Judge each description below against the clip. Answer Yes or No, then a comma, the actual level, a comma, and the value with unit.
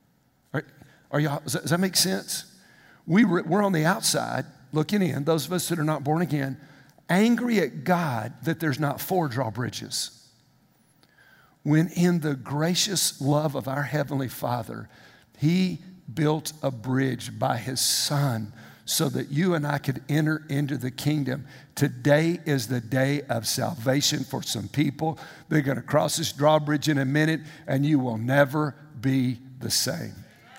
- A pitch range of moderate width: Yes, average, 3.0 semitones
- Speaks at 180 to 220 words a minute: No, average, 155 wpm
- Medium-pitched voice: Yes, medium, 150 Hz